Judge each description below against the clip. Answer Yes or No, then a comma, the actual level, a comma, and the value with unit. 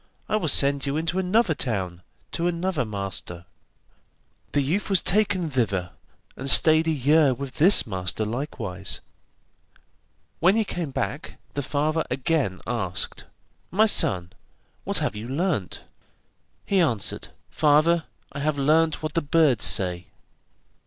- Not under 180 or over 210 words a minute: No, slow, 135 wpm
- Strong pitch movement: Yes, wide, 6.9 semitones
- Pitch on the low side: No, medium, 145 Hz